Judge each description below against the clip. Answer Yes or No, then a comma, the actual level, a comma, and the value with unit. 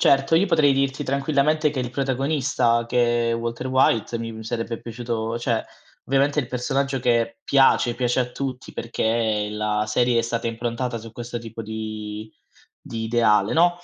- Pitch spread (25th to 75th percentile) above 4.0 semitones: No, average, 2.8 semitones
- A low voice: Yes, low, 120 Hz